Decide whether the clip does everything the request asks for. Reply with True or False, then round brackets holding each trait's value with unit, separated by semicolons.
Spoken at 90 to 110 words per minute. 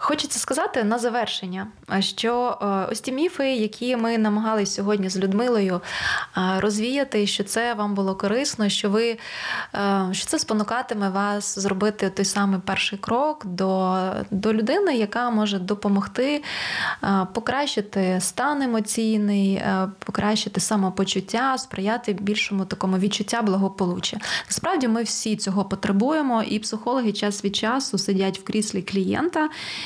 False (125 wpm)